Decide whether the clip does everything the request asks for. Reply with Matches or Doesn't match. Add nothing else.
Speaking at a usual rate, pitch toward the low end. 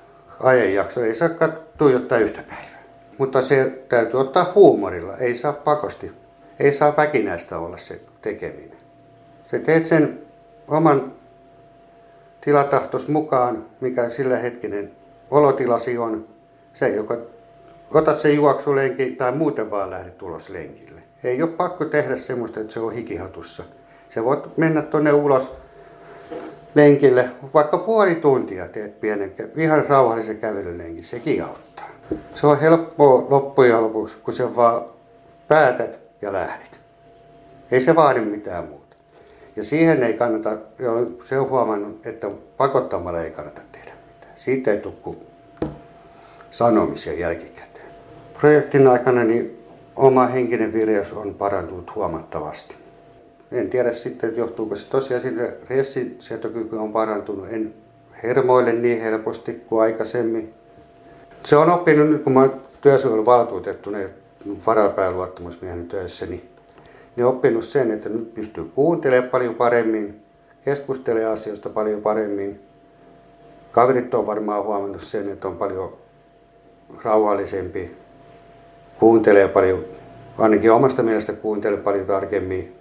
Matches